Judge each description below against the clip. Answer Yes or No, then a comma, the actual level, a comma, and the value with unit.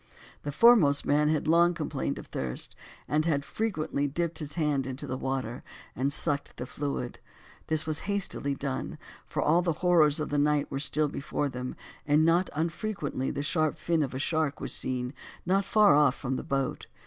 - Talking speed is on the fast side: No, average, 185 wpm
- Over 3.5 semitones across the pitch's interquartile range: No, average, 3.0 semitones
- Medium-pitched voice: Yes, medium, 150 Hz